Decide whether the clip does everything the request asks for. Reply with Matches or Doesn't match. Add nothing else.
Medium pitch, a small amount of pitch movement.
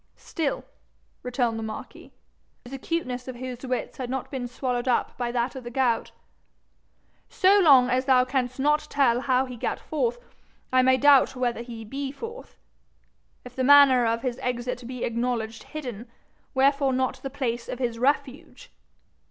Doesn't match